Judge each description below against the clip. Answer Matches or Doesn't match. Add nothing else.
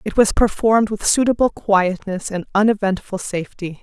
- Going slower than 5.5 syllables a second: Matches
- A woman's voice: Matches